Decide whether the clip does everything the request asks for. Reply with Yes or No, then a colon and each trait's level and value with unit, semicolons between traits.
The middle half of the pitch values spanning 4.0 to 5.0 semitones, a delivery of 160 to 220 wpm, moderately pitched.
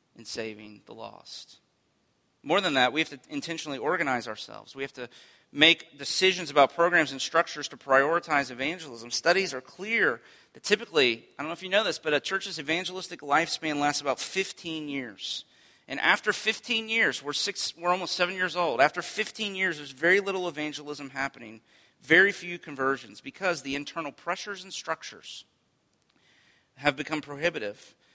Yes: average, 4.6 semitones; average, 165 wpm; medium, 155 Hz